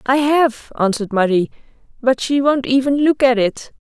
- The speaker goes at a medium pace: Yes, average, 175 wpm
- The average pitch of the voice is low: No, very high, 255 Hz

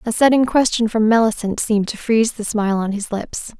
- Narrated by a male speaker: No, female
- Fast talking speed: Yes, fast, 215 wpm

